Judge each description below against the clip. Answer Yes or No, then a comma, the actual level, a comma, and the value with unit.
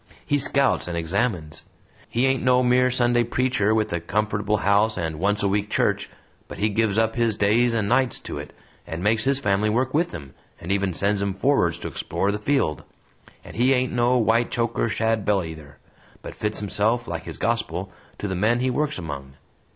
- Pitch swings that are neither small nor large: Yes, average, 3.8 semitones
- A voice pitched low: Yes, low, 105 Hz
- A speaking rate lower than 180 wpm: No, average, 195 wpm